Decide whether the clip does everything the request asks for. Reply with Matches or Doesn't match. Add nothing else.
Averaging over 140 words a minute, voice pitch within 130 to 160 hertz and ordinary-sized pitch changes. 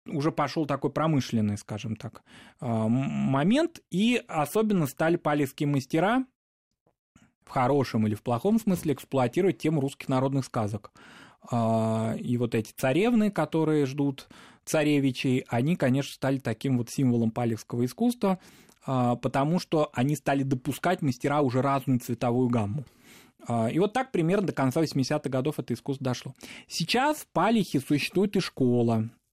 Doesn't match